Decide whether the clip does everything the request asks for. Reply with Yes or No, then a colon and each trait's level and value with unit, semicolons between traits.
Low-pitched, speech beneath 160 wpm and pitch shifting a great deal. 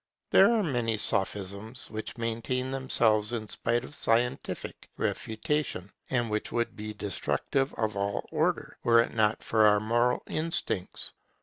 No: low, 115 Hz; average, 140 wpm; narrow, 2.6 semitones